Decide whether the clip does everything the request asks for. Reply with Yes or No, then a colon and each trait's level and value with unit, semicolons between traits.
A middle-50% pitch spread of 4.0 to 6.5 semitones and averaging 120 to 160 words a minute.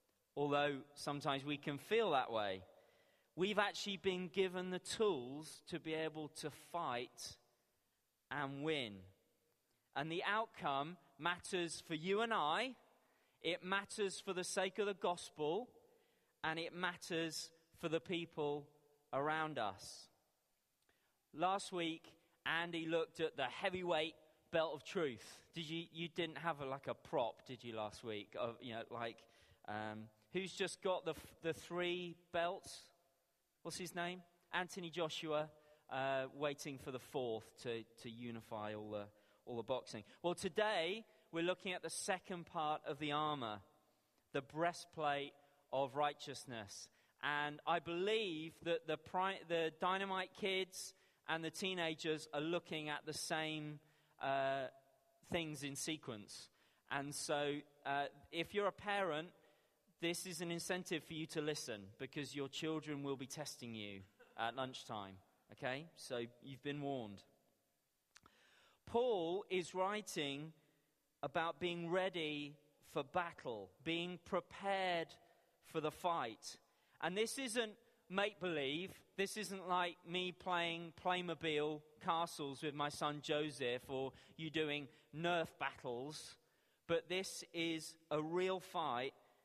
No: average, 3.6 semitones; average, 140 wpm